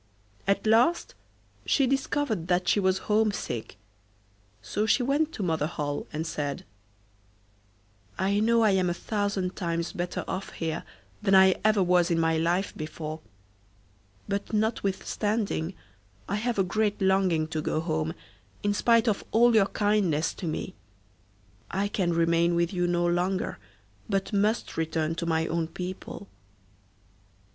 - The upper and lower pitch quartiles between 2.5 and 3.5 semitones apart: No, average, 3.9 semitones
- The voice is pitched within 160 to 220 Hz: Yes, high, 190 Hz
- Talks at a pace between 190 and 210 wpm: No, average, 145 wpm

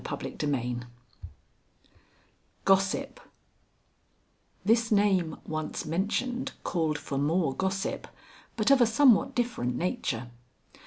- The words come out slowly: Yes, slow, 90 wpm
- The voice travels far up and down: Yes, wide, 7.4 semitones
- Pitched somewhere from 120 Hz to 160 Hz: No, high, 190 Hz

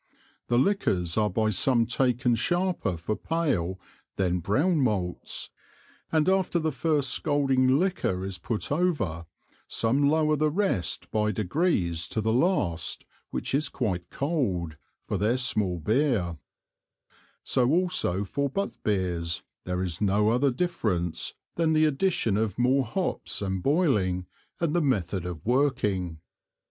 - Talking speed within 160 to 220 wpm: No, slow, 135 wpm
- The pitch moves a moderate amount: No, wide, 8.4 semitones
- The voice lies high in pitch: No, low, 120 Hz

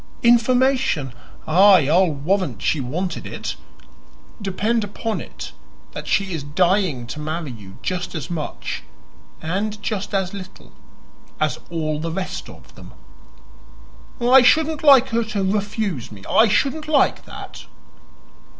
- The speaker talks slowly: Yes, slow, 130 wpm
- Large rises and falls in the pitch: Yes, wide, 6.2 semitones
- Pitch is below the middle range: No, high, 190 Hz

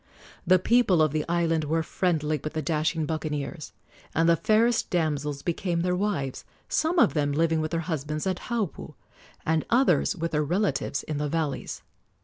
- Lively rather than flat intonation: No, average, 3.0 semitones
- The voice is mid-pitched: Yes, medium, 160 Hz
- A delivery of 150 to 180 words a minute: Yes, average, 170 wpm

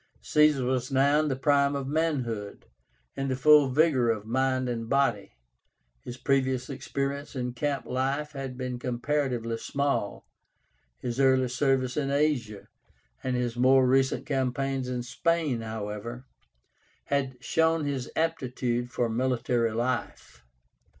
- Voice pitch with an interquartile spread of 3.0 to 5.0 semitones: No, narrow, 2.4 semitones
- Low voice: Yes, low, 130 Hz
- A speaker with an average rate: No, slow, 130 wpm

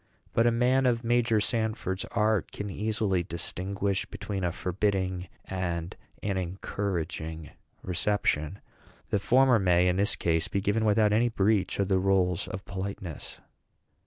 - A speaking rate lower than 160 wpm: Yes, average, 140 wpm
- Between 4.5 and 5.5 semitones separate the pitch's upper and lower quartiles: No, average, 3.1 semitones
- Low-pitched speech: Yes, low, 100 Hz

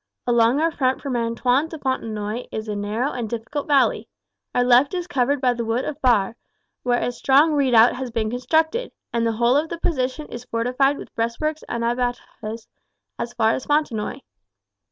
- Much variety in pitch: No, average, 3.6 semitones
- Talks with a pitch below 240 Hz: No, high, 245 Hz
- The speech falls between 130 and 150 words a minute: No, average, 180 wpm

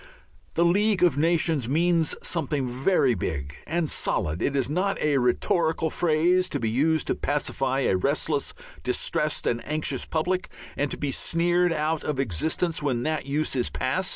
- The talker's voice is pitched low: No, medium, 150 Hz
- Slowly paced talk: No, average, 170 wpm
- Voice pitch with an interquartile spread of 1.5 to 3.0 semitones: No, average, 4.2 semitones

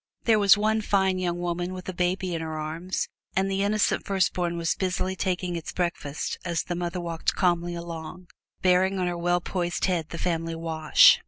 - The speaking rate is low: No, average, 190 wpm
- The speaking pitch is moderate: Yes, medium, 175 Hz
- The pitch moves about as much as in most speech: No, narrow, 1.7 semitones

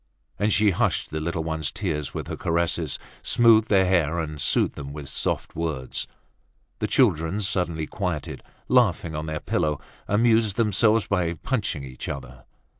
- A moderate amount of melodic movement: Yes, average, 5.0 semitones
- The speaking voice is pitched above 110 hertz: No, very low, 85 Hz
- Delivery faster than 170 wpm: No, average, 155 wpm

